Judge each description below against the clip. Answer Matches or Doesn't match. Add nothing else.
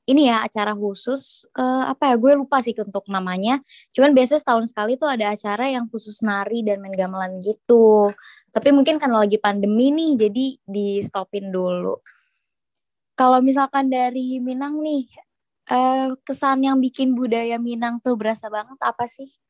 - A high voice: Matches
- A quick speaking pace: Matches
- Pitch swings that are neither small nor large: Matches